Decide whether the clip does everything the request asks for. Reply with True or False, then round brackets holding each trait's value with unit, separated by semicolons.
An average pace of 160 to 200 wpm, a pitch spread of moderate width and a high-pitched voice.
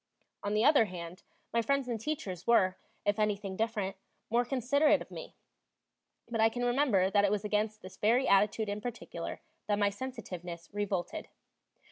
True (165 wpm; 3.4 semitones; 210 Hz)